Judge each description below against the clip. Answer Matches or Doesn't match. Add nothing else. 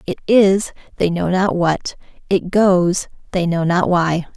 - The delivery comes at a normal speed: Matches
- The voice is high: Doesn't match